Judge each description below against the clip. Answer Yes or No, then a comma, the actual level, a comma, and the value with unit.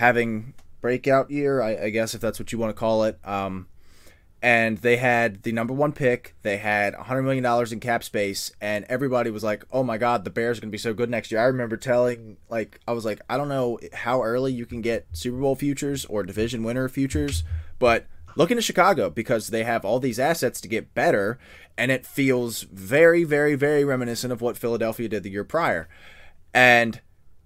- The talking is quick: Yes, fast, 210 wpm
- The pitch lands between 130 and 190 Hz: No, low, 115 Hz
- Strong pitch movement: No, average, 2.9 semitones